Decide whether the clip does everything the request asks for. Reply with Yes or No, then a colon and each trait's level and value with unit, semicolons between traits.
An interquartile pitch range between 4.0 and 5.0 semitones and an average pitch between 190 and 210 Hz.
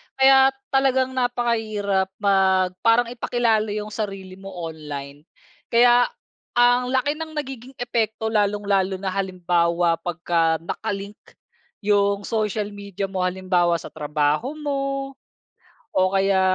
Yes: average, 4.6 semitones; high, 205 Hz